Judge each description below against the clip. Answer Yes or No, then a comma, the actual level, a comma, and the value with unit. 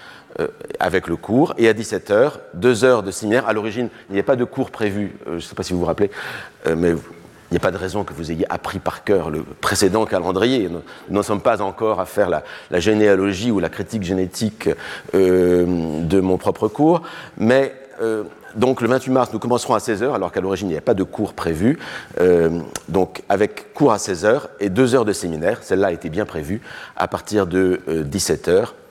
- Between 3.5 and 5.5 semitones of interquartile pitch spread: Yes, average, 5.1 semitones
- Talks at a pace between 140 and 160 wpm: No, fast, 220 wpm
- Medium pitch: No, low, 100 Hz